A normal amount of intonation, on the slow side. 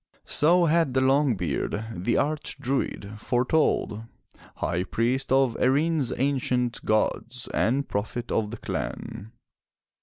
Yes: average, 3.9 semitones; slow, 125 wpm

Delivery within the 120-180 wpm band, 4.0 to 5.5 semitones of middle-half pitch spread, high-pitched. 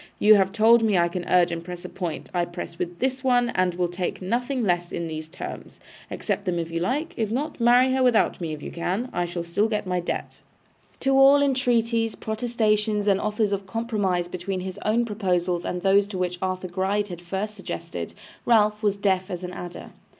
No: fast, 205 wpm; average, 4.3 semitones; high, 195 Hz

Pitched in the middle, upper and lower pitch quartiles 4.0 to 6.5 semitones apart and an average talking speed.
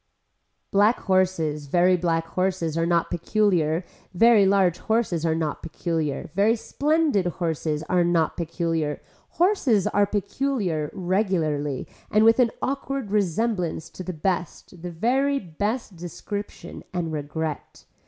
No: medium, 180 Hz; average, 4.5 semitones; slow, 125 wpm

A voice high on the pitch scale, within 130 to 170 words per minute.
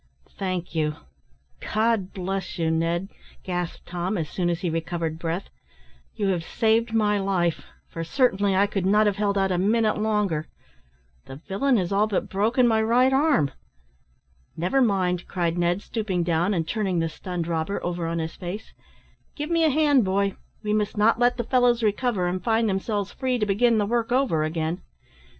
No: high, 195 Hz; average, 180 wpm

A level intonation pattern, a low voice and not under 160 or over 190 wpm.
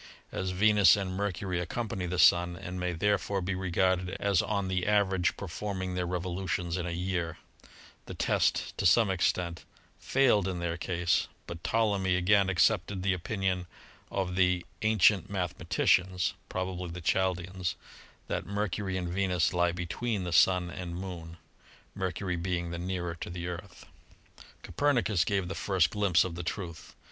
Yes: narrow, 1.9 semitones; very low, 90 Hz; average, 170 wpm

